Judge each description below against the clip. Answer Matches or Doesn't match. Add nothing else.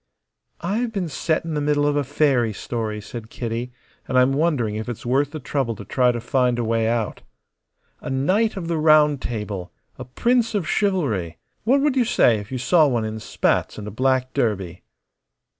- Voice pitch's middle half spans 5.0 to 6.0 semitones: Matches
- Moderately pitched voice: Doesn't match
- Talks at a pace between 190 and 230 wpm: Matches